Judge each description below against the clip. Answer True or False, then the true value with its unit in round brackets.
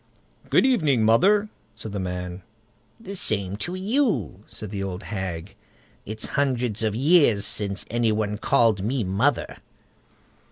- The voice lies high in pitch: False (110 Hz)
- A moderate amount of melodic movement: False (6.4 semitones)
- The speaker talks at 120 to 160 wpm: True (135 wpm)